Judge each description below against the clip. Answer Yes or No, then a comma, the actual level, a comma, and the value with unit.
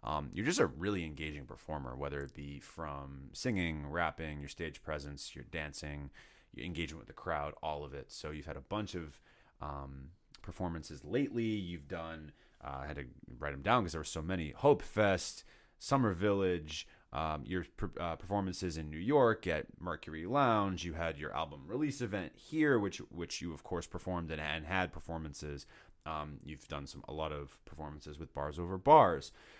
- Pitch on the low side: Yes, very low, 80 Hz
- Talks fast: No, average, 180 wpm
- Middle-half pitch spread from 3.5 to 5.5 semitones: Yes, average, 3.8 semitones